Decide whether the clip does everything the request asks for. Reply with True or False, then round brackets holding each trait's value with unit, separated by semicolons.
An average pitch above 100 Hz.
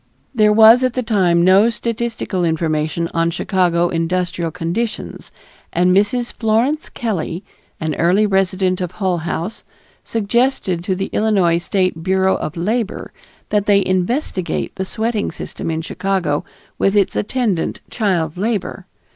True (190 Hz)